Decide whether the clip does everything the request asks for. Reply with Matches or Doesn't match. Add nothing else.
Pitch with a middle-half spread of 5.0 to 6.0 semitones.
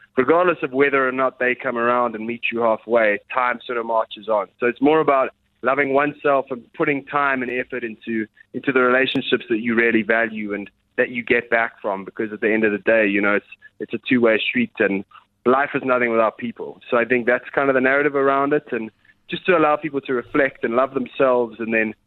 Doesn't match